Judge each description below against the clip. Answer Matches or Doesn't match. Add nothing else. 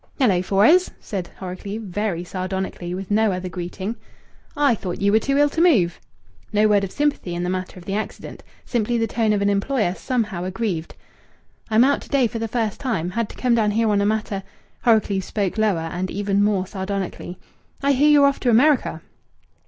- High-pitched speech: Matches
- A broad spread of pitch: Doesn't match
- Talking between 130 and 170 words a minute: Doesn't match